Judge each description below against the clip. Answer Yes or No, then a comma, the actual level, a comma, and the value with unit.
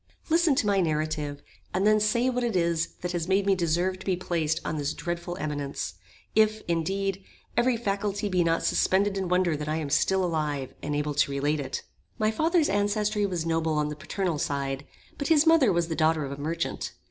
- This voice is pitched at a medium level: Yes, medium, 175 Hz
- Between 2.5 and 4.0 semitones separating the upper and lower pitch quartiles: No, average, 4.9 semitones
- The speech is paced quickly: Yes, fast, 210 wpm